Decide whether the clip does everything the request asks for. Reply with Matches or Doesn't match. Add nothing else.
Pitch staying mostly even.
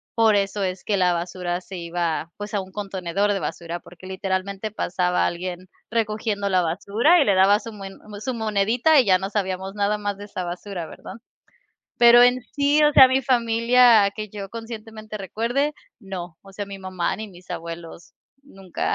Doesn't match